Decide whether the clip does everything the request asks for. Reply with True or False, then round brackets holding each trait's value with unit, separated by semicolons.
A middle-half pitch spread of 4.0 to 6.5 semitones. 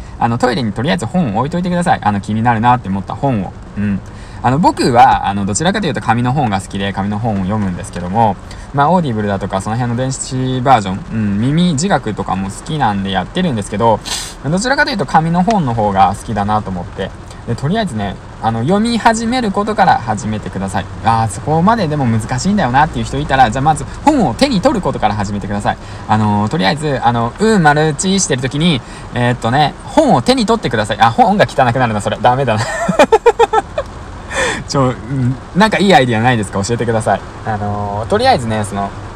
False (7.4 semitones)